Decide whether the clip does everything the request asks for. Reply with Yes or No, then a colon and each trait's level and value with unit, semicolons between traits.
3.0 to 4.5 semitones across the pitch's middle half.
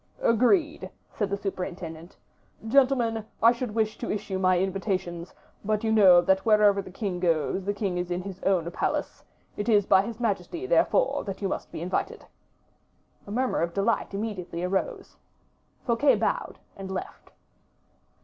Yes: average, 3.4 semitones